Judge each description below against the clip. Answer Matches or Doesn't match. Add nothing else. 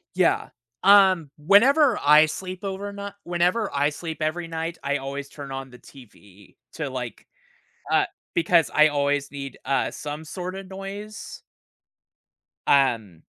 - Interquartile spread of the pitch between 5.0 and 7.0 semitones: Matches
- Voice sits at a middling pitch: Matches